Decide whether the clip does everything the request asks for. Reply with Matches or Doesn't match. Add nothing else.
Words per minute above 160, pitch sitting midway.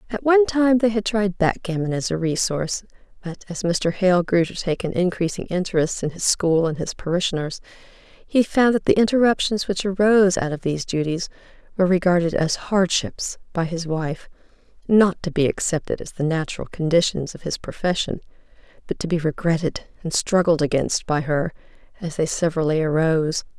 Matches